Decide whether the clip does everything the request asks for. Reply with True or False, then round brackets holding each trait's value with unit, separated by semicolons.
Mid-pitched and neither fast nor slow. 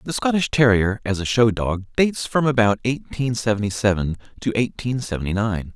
False (110 Hz; 175 wpm)